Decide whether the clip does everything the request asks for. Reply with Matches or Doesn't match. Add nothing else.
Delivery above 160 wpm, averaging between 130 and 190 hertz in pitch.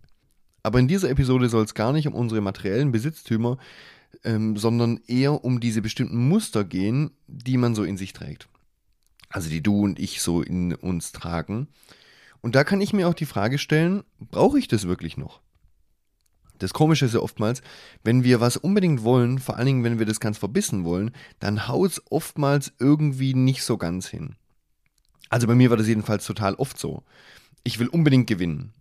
Doesn't match